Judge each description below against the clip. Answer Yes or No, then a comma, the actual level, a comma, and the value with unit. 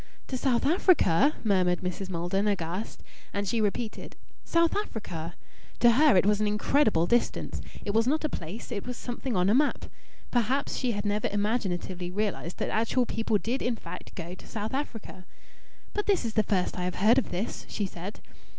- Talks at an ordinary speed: Yes, average, 185 wpm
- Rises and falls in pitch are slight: No, average, 4.8 semitones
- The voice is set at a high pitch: Yes, high, 215 Hz